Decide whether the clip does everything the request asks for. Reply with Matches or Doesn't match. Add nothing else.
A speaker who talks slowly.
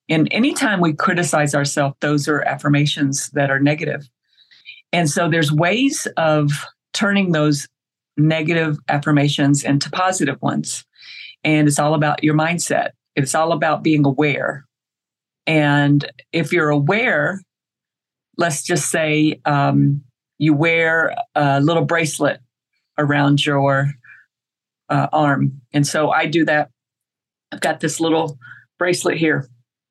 Matches